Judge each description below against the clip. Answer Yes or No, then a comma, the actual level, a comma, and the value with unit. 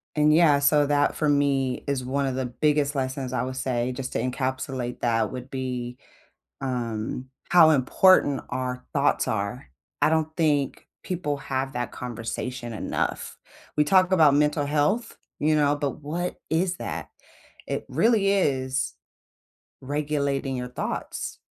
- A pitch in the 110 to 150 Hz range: Yes, medium, 140 Hz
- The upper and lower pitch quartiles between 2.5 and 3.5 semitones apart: Yes, average, 2.9 semitones